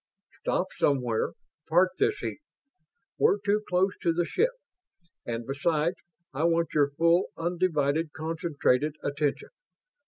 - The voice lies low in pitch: No, medium, 165 Hz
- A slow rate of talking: Yes, slow, 120 wpm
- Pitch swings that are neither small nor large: Yes, average, 3.7 semitones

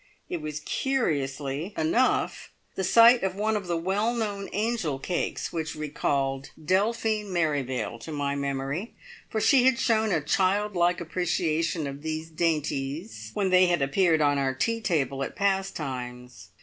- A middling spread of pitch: No, wide, 6.0 semitones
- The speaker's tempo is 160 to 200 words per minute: No, average, 150 wpm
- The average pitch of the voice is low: No, medium, 165 Hz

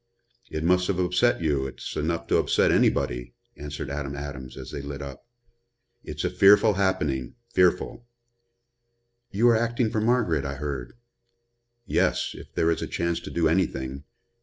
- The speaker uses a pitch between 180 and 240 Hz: No, very low, 80 Hz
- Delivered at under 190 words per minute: Yes, average, 160 wpm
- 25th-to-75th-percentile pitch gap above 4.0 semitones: Yes, average, 5.2 semitones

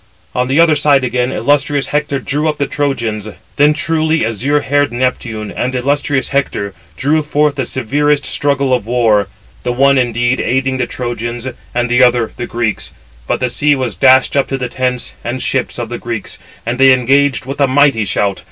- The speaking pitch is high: No, low, 130 Hz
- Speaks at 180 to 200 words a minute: Yes, average, 190 wpm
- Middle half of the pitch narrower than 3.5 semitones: Yes, average, 2.9 semitones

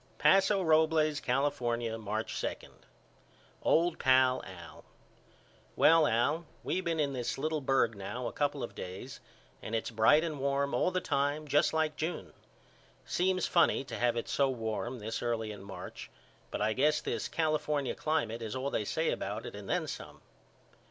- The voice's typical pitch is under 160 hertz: Yes, medium, 140 Hz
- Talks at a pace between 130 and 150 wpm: No, average, 165 wpm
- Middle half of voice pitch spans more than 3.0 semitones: Yes, average, 5.0 semitones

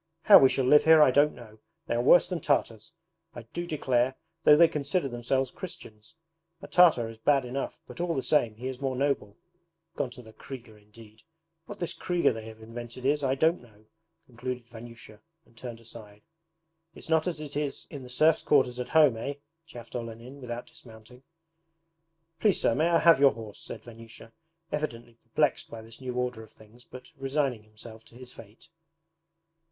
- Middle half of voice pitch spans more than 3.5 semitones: Yes, average, 4.1 semitones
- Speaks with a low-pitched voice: Yes, low, 125 Hz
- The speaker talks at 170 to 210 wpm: Yes, average, 190 wpm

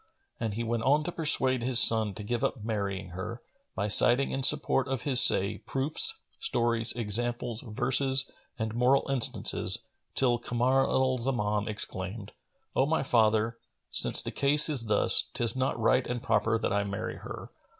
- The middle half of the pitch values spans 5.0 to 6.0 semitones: No, average, 3.3 semitones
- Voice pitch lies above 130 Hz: No, low, 120 Hz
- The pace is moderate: Yes, average, 165 wpm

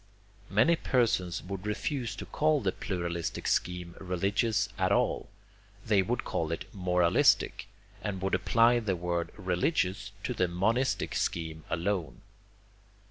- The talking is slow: Yes, slow, 130 wpm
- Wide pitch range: No, average, 4.1 semitones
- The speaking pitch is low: Yes, very low, 95 Hz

